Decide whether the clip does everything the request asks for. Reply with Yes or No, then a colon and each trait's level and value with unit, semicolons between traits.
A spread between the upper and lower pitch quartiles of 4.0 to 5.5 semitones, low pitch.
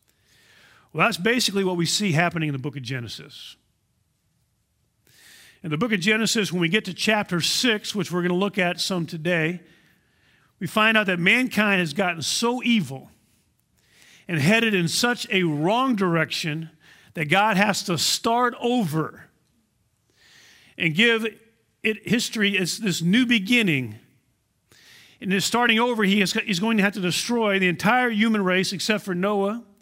No: average, 4.8 semitones; high, 195 Hz